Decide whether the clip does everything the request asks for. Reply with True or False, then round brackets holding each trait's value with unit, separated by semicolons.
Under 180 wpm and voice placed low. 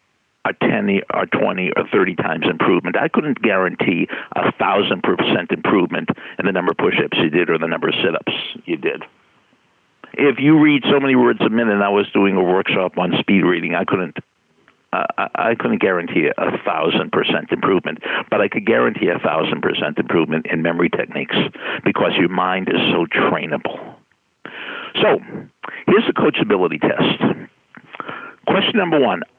True (170 wpm; 110 Hz)